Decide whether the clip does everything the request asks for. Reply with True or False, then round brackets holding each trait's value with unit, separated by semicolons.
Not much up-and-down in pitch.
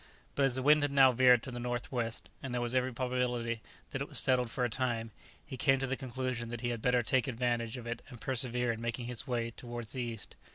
True (1.6 semitones)